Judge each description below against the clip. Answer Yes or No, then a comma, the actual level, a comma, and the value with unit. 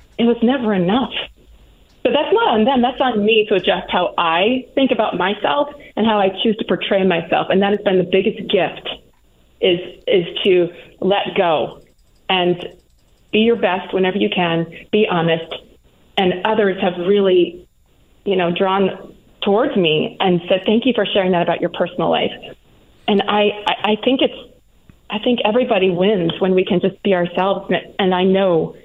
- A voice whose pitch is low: No, high, 195 Hz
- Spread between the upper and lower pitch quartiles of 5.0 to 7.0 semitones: No, average, 3.2 semitones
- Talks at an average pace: Yes, average, 180 wpm